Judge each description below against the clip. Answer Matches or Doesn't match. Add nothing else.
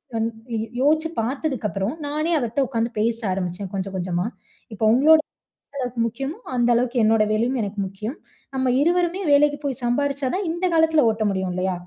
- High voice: Matches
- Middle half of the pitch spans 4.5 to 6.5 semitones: Matches